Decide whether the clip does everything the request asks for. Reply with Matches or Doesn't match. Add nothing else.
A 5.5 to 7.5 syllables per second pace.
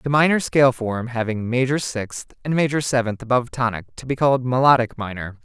Matches